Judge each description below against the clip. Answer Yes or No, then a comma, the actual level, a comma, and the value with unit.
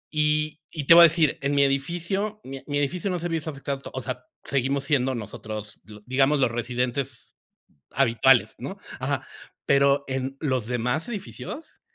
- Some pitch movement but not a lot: Yes, average, 3.2 semitones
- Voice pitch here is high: No, medium, 140 Hz